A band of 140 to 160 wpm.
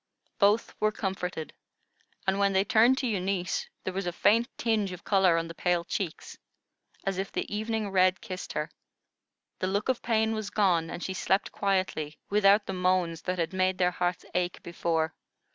No: average, 180 wpm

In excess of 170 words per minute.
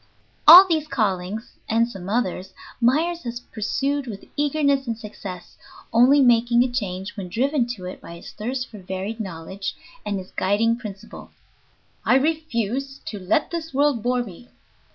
No: average, 155 wpm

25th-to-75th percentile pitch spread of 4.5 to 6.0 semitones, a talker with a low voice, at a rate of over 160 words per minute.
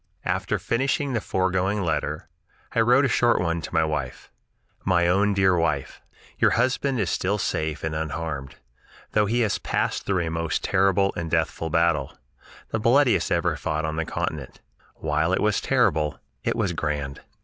Yes: average, 4.9 semitones; very low, 85 Hz; average, 170 wpm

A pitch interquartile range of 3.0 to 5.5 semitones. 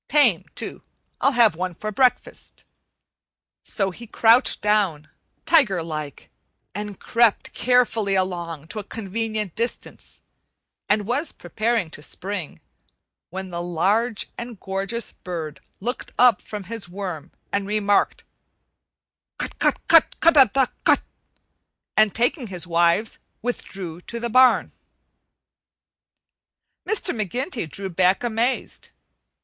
Yes: average, 4.7 semitones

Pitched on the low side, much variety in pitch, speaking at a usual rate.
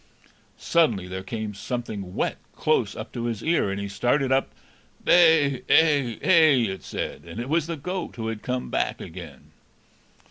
Yes: low, 125 Hz; wide, 6.9 semitones; average, 170 wpm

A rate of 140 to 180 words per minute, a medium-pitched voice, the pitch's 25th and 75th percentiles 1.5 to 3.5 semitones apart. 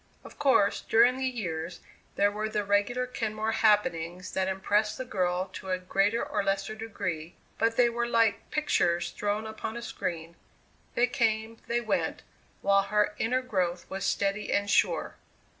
No: average, 160 wpm; high, 210 Hz; average, 3.2 semitones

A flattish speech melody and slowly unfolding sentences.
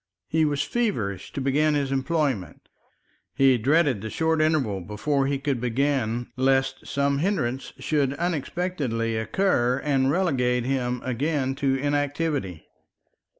No: average, 3.4 semitones; slow, 125 wpm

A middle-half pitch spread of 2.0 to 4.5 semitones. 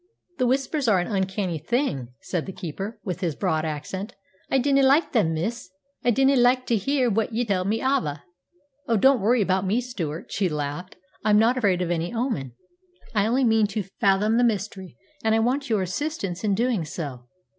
No: average, 5.3 semitones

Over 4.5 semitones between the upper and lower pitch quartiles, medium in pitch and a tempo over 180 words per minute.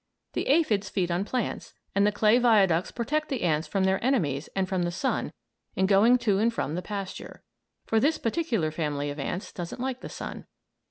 No: wide, 5.4 semitones; high, 200 Hz; average, 200 wpm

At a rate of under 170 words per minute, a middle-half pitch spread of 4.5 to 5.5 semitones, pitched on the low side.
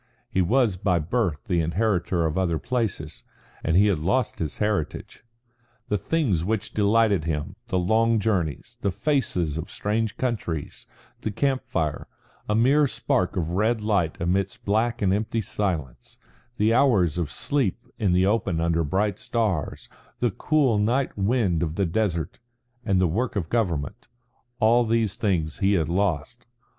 Yes: average, 160 wpm; average, 4.9 semitones; low, 100 Hz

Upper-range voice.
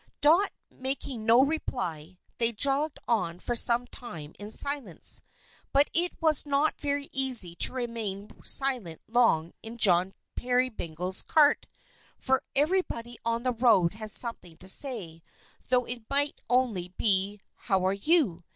Yes: high, 235 Hz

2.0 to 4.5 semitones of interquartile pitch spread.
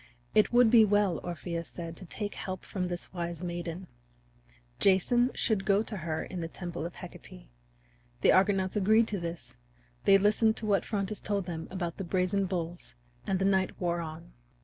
Yes: average, 2.9 semitones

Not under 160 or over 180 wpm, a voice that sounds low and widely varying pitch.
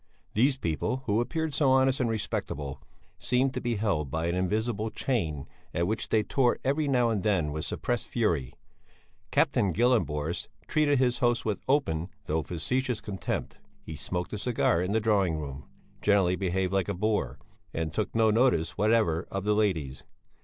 Yes: average, 170 wpm; low, 105 Hz; wide, 6.4 semitones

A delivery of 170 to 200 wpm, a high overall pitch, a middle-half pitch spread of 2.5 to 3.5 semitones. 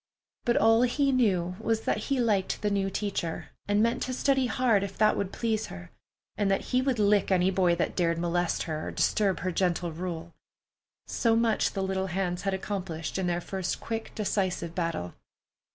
No: average, 190 wpm; high, 195 Hz; average, 4.0 semitones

